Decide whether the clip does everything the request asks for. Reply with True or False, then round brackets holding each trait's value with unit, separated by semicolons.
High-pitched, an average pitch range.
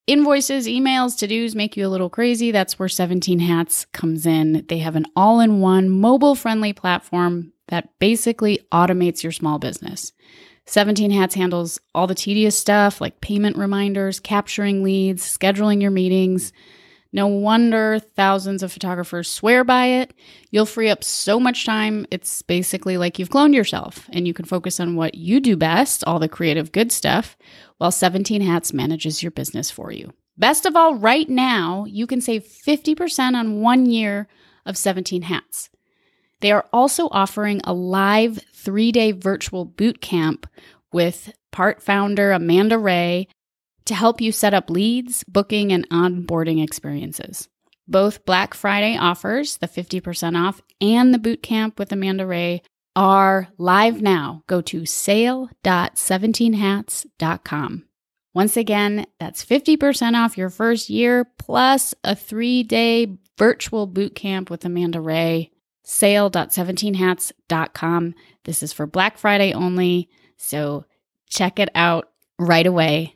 True (195 Hz; 4.0 semitones)